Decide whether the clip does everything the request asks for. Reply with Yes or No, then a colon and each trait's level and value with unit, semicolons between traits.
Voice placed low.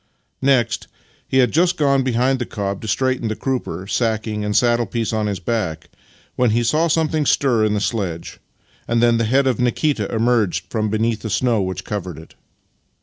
Yes: low, 115 Hz